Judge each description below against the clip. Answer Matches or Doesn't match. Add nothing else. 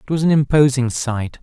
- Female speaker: Doesn't match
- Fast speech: Matches